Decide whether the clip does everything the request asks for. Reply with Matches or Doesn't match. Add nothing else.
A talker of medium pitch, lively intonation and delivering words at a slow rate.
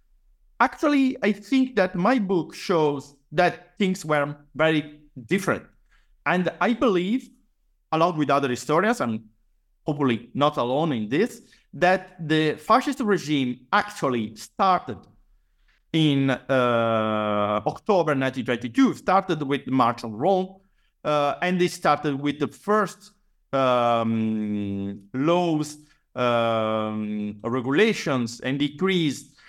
Matches